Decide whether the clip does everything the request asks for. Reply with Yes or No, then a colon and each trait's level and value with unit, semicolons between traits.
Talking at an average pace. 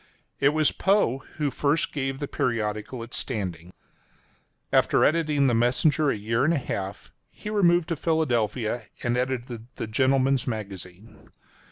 Yes: average, 155 wpm